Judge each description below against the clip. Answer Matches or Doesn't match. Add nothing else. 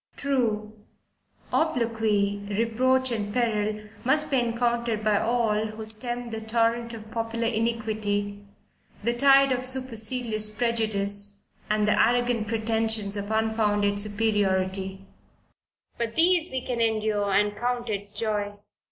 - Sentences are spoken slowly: Matches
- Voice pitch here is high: Matches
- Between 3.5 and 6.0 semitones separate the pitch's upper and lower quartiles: Doesn't match